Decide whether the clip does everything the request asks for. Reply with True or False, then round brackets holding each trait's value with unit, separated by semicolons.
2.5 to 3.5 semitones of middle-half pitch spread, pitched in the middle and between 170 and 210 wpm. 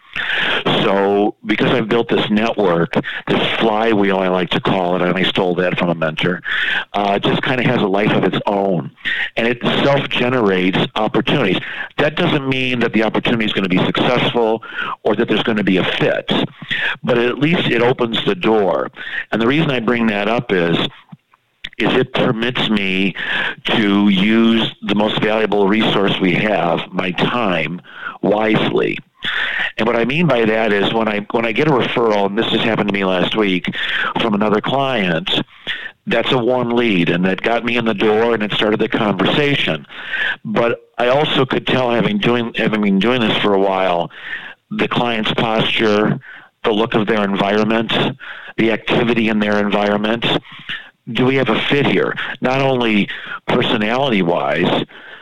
False (3.2 semitones; 110 Hz; 175 wpm)